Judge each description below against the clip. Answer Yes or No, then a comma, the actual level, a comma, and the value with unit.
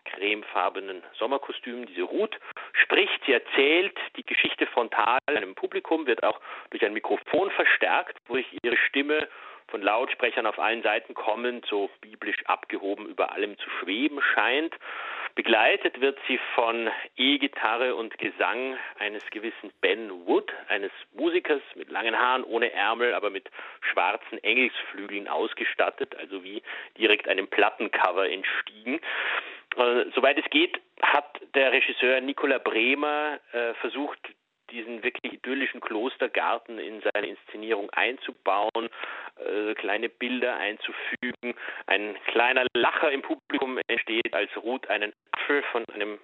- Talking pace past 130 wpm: No, slow, 125 wpm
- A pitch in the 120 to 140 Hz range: No, very high, 305 Hz